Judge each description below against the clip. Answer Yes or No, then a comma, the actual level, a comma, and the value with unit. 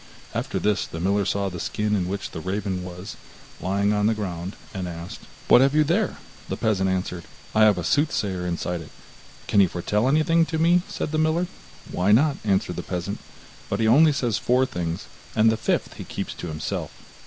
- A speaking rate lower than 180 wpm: No, average, 200 wpm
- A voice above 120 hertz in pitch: No, low, 100 Hz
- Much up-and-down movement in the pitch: Yes, wide, 5.9 semitones